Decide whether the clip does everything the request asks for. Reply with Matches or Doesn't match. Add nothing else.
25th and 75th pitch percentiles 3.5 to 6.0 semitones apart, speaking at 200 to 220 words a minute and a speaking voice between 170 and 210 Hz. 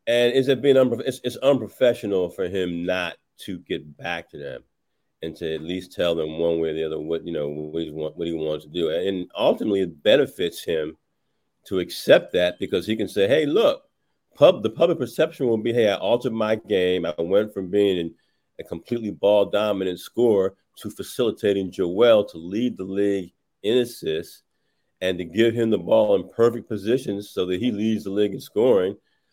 Doesn't match